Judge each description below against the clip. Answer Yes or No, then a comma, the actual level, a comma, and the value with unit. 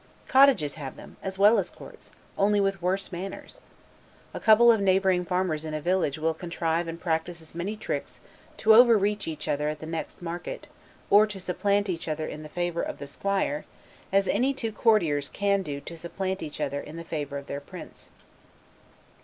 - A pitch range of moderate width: Yes, average, 4.1 semitones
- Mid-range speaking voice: Yes, medium, 180 Hz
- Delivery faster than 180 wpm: Yes, average, 195 wpm